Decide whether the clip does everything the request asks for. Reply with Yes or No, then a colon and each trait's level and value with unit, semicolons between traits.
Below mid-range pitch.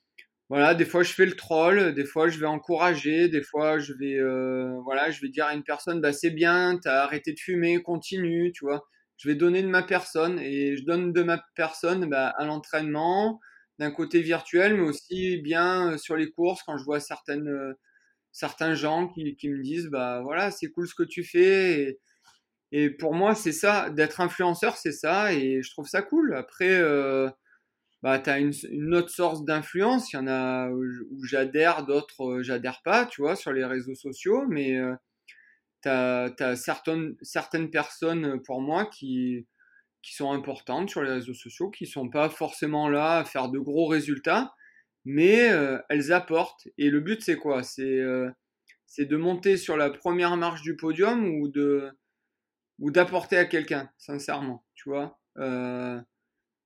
No: medium, 155 Hz